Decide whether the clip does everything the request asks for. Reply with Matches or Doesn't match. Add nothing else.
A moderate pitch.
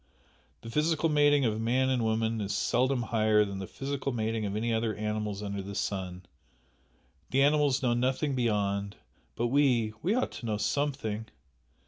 Doesn't match